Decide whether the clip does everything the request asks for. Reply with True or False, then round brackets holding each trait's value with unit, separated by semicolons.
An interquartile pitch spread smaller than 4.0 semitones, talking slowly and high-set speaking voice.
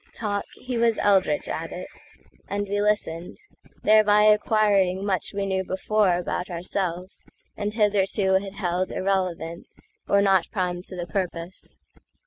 True (2.4 semitones; 120 wpm; 195 Hz)